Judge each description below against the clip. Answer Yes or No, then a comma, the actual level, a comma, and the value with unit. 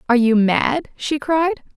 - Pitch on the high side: Yes, very high, 275 Hz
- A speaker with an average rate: Yes, average, 170 wpm